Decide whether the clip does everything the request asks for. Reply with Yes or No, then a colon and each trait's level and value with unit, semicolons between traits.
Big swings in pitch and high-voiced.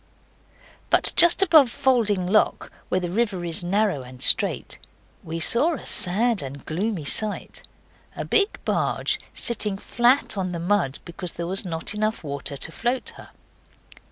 Yes: wide, 5.9 semitones; high, 195 Hz